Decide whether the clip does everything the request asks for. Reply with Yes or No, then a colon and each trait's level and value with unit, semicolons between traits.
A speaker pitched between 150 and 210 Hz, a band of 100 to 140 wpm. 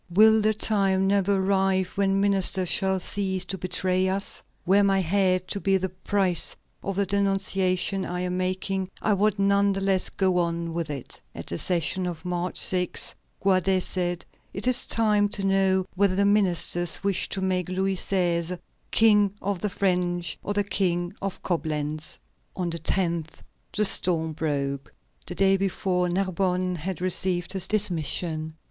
No: high, 190 Hz; average, 165 wpm